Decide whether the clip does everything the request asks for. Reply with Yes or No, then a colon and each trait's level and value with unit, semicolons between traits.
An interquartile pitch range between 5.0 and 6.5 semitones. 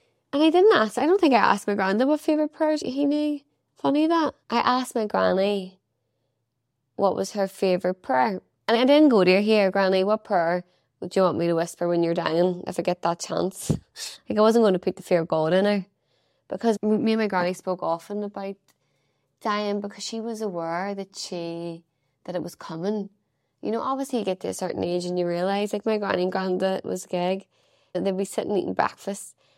No: average, 3.6 semitones